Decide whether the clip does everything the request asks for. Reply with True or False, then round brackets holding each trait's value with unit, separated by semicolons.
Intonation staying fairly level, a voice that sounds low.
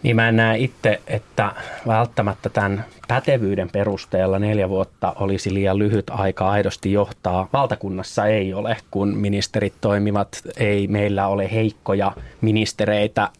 True (1.8 semitones; 100 Hz)